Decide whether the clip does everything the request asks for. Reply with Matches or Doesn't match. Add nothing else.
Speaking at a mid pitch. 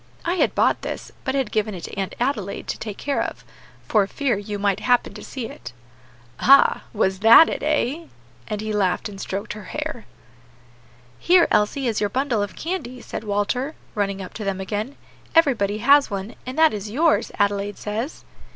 Doesn't match